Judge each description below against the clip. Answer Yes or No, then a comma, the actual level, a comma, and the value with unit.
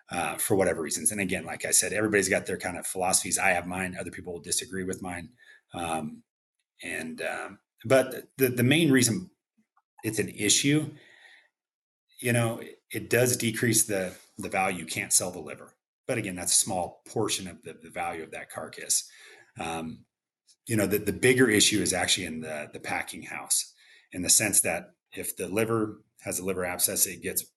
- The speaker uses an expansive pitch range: Yes, wide, 5.7 semitones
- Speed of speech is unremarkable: Yes, average, 195 wpm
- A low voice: Yes, low, 110 Hz